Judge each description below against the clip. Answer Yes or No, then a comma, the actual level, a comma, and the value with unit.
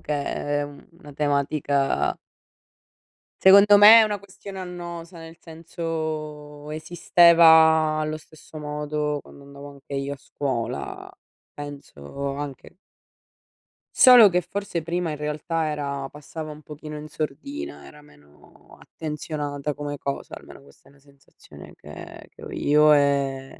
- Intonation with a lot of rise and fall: No, narrow, 2.5 semitones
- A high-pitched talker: No, medium, 150 Hz